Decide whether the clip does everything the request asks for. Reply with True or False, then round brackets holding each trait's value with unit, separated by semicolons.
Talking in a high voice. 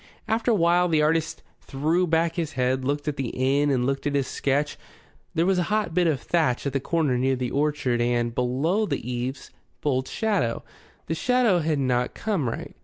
False (145 Hz)